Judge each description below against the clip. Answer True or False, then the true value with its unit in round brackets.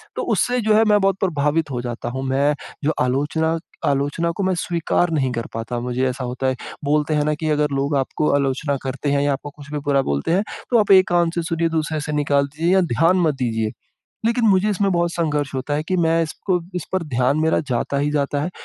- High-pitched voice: False (150 Hz)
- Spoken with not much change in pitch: False (3.7 semitones)